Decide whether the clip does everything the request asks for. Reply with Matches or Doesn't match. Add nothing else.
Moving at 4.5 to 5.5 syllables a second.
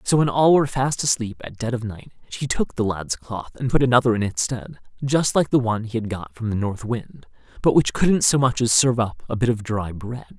Matches